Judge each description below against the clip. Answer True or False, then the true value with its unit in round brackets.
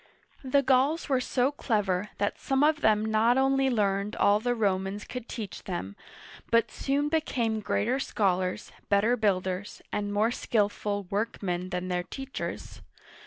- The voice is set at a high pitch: True (215 Hz)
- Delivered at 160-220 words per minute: False (150 wpm)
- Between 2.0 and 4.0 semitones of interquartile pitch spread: False (4.4 semitones)